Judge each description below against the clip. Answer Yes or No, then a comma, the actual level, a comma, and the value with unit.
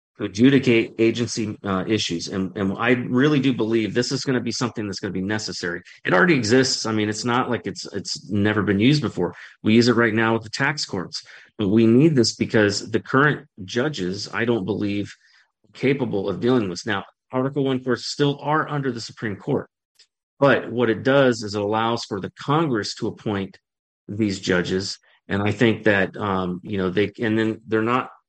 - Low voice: Yes, low, 110 Hz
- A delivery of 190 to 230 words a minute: Yes, fast, 205 wpm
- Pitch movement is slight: No, average, 3.5 semitones